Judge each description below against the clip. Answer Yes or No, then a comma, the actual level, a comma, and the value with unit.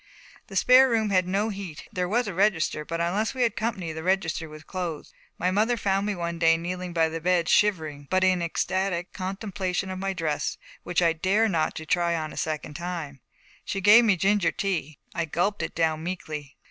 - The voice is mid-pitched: Yes, medium, 180 Hz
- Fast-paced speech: Yes, fast, 210 wpm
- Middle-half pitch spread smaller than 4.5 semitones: Yes, average, 3.2 semitones